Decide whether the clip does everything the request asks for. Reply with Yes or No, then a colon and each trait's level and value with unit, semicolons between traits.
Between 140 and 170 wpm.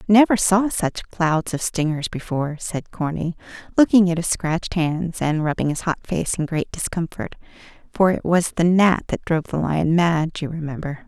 No: average, 180 wpm